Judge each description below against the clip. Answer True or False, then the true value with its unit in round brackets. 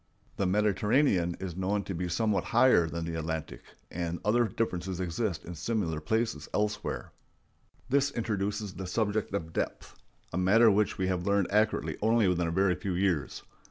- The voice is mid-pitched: False (95 Hz)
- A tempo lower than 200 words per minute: True (160 wpm)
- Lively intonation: False (3.6 semitones)